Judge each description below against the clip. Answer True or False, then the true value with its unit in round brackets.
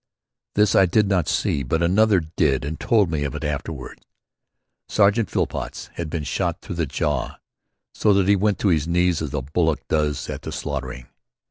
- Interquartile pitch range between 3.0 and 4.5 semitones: False (4.9 semitones)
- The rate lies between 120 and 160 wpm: False (190 wpm)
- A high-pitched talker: False (85 Hz)